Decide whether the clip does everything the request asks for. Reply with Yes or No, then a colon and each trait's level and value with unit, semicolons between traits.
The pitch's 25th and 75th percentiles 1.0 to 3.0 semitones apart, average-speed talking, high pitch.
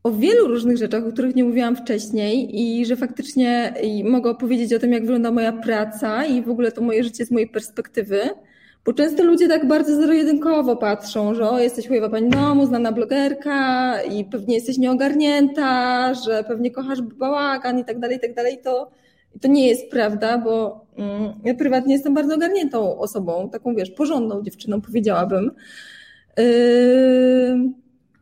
No: average, 2.7 semitones; fast, 165 wpm; high, 245 Hz